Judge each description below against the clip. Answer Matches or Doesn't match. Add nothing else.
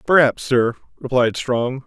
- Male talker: Matches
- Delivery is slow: Matches